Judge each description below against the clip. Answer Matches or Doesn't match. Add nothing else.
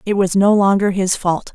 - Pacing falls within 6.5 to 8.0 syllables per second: Doesn't match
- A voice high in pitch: Matches